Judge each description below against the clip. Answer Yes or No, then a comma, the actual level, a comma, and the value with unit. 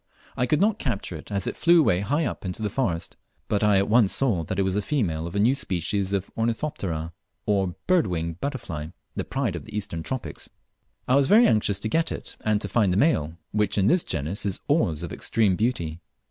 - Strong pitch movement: Yes, wide, 6.1 semitones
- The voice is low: Yes, low, 100 Hz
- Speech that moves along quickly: Yes, fast, 225 wpm